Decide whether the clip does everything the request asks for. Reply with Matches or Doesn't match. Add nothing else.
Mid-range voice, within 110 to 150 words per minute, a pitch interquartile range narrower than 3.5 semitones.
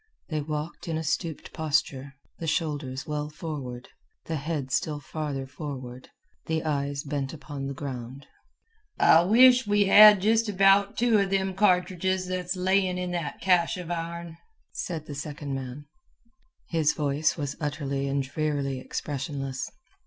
Doesn't match